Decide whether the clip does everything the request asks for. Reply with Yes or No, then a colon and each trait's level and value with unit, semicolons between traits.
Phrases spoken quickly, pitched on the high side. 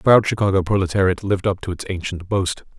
No: fast, 215 wpm; very low, 95 Hz